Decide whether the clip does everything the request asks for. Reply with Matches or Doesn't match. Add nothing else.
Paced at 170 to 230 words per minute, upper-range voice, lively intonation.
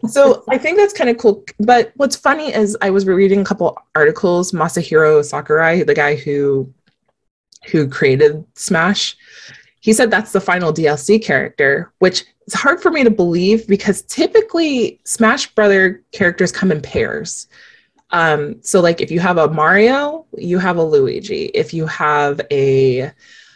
Doesn't match